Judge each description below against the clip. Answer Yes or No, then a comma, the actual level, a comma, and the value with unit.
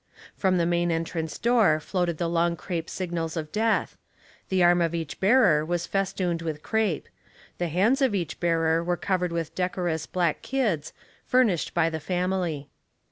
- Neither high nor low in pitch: Yes, medium, 175 Hz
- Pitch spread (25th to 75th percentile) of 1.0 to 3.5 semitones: Yes, narrow, 2.4 semitones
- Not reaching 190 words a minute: Yes, average, 170 wpm